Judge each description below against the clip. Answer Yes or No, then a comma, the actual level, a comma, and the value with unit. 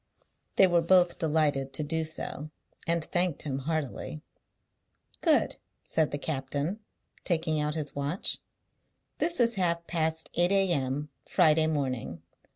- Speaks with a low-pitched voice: No, medium, 160 Hz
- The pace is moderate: No, slow, 130 wpm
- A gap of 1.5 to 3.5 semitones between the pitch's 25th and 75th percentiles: Yes, average, 3.2 semitones